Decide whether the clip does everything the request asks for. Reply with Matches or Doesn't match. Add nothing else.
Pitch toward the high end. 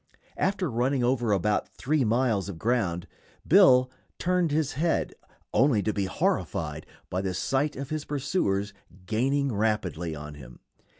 Doesn't match